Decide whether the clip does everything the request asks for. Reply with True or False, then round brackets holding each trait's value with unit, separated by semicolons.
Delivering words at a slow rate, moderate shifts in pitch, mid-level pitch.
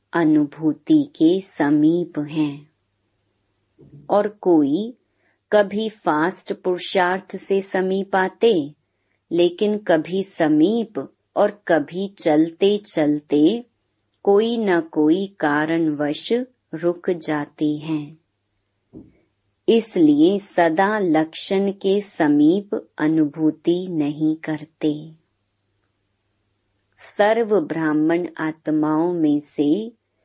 True (75 wpm; 4.9 semitones; 160 Hz)